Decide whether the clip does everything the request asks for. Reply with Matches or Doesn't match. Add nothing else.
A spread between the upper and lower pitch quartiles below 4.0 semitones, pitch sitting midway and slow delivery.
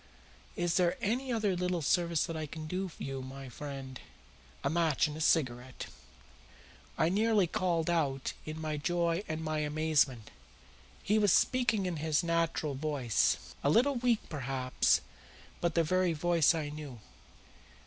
Doesn't match